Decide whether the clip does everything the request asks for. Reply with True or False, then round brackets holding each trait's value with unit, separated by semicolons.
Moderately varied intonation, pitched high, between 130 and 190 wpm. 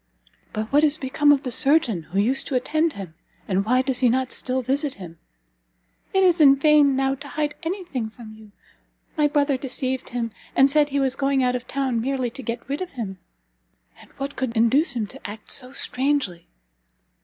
False (3.5 semitones; 265 Hz; 200 wpm)